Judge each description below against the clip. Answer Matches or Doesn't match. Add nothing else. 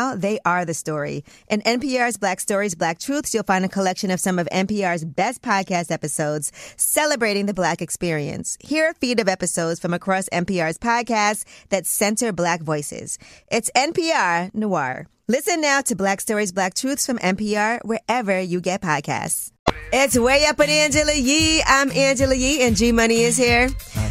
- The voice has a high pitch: Matches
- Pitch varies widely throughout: Matches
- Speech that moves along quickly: Doesn't match